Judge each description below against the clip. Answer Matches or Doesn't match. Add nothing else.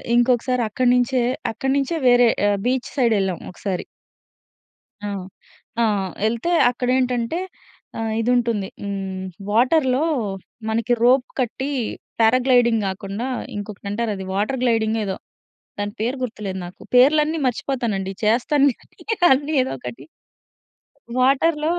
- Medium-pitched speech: Doesn't match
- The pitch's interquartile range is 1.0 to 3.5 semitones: Doesn't match